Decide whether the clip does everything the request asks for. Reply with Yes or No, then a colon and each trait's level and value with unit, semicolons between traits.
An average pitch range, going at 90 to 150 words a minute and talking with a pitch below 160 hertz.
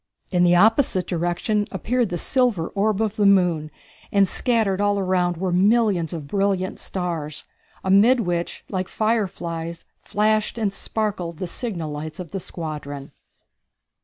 No: average, 3.7 semitones; average, 140 wpm; high, 190 Hz